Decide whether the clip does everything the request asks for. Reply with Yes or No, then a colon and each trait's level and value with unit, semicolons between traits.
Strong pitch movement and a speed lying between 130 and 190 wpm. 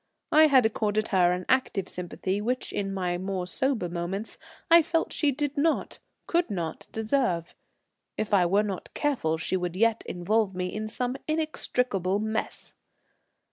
Yes: wide, 5.9 semitones; average, 155 wpm